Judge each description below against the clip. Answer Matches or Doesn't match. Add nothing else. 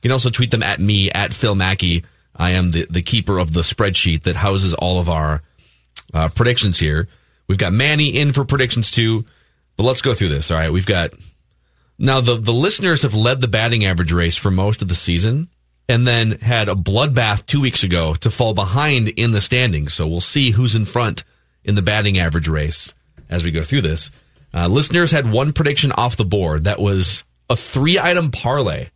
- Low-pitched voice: Matches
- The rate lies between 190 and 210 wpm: Matches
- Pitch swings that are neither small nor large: Doesn't match